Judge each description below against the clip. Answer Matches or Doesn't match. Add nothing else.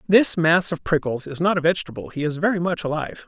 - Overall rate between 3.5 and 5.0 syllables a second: Doesn't match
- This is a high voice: Doesn't match